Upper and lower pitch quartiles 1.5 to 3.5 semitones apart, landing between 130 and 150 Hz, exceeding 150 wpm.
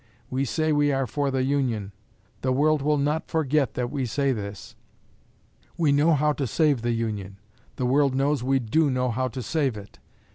Yes: average, 3.2 semitones; low, 135 Hz; average, 190 wpm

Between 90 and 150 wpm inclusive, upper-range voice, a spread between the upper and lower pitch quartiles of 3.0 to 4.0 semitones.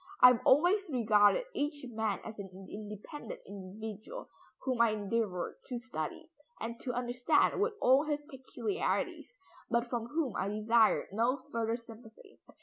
Yes: average, 145 wpm; high, 235 Hz; average, 3.7 semitones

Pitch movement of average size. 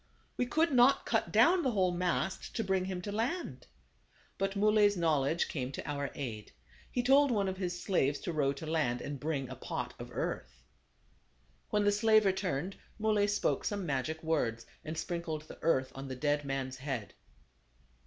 No: wide, 6.6 semitones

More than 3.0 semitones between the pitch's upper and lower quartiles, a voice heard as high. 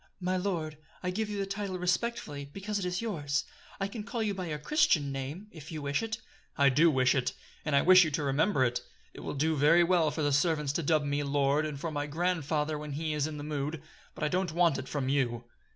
No: average, 4.1 semitones; medium, 155 Hz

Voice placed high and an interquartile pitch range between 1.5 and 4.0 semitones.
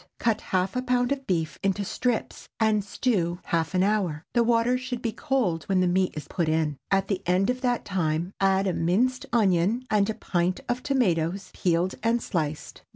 No: high, 195 Hz; average, 5.3 semitones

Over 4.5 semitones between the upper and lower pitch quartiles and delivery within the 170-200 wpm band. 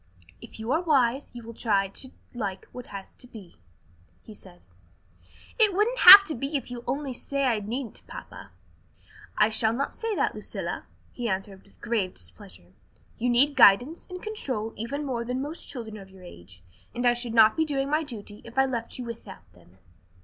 Yes: average, 5.2 semitones; average, 195 wpm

